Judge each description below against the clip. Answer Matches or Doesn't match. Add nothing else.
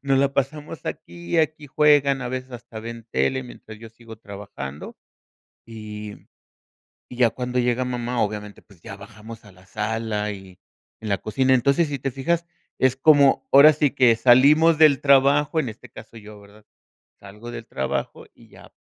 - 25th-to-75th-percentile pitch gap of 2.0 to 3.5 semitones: Doesn't match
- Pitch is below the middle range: Matches